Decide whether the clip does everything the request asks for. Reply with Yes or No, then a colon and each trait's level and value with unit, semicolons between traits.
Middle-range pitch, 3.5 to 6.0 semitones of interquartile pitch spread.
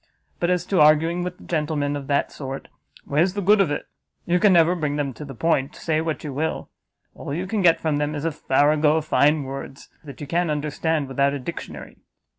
No: medium, 150 Hz; average, 2.9 semitones